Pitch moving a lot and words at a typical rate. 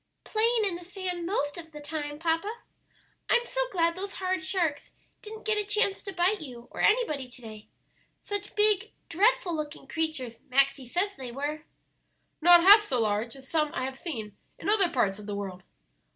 Yes: wide, 6.8 semitones; average, 185 wpm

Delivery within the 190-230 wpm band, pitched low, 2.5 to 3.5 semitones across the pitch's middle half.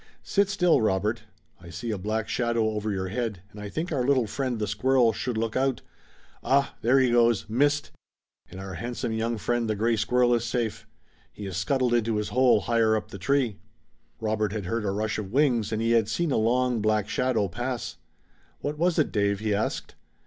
Yes: fast, 205 wpm; low, 115 Hz; average, 3.1 semitones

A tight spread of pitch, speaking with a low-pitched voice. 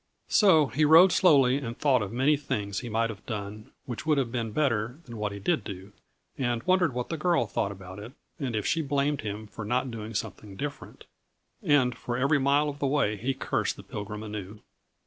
No: average, 5.3 semitones; low, 125 Hz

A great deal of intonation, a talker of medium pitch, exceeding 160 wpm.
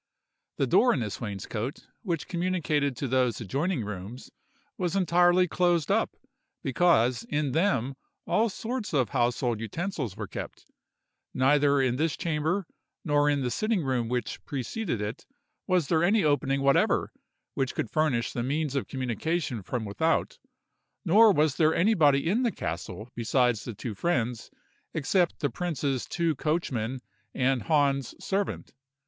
No: wide, 5.9 semitones; medium, 145 Hz; average, 145 wpm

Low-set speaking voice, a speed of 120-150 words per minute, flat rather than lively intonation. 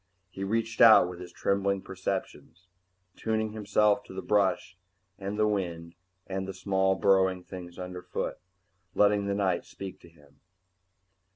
Yes: very low, 95 Hz; average, 145 wpm; narrow, 2.0 semitones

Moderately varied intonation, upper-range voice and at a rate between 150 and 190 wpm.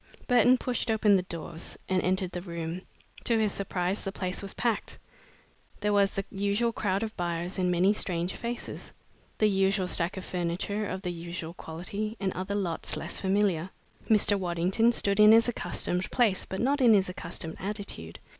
Yes: average, 3.0 semitones; high, 195 Hz; average, 175 wpm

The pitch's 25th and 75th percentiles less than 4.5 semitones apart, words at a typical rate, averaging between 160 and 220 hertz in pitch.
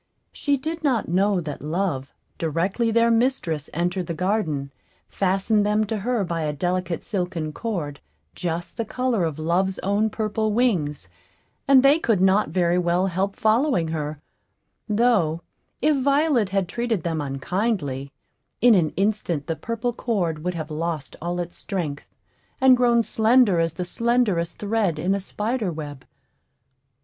No: wide, 5.5 semitones; average, 150 wpm; high, 190 Hz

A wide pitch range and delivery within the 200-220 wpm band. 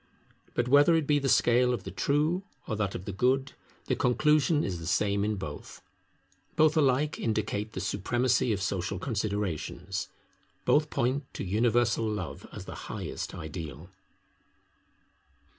No: wide, 5.7 semitones; average, 145 wpm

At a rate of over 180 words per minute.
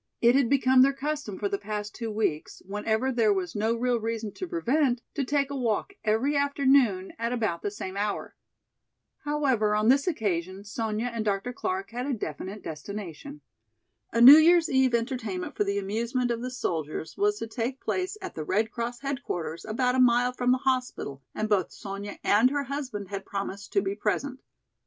Yes: average, 190 wpm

